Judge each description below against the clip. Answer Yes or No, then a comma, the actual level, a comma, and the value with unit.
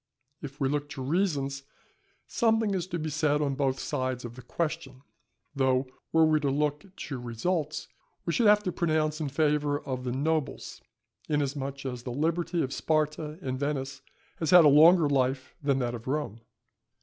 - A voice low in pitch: No, medium, 145 Hz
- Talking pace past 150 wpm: Yes, average, 175 wpm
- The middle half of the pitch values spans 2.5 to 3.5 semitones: Yes, average, 3.0 semitones